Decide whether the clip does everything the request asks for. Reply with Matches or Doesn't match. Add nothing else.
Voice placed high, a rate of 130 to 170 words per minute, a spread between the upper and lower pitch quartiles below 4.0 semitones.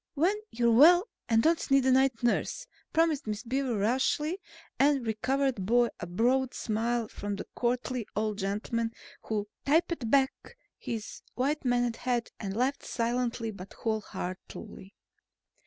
Matches